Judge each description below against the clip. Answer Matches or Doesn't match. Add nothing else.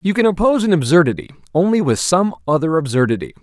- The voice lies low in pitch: Doesn't match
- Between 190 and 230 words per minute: Doesn't match